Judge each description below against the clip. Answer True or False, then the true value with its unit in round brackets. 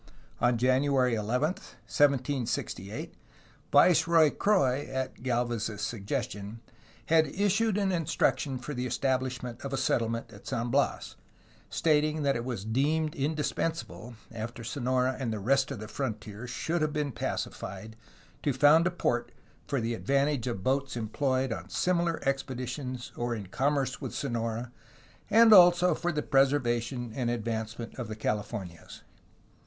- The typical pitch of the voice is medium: False (130 Hz)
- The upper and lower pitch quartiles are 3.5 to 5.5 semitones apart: True (4.0 semitones)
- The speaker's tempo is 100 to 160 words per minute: True (145 wpm)